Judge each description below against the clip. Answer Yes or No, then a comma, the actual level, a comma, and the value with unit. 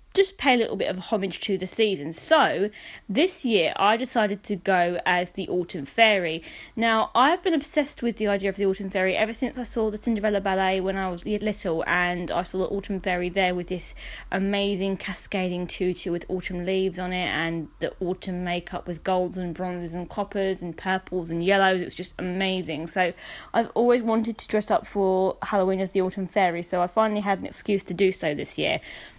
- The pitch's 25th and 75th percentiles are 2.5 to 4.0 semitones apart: Yes, average, 3.0 semitones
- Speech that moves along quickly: Yes, fast, 210 wpm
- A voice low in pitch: No, high, 190 Hz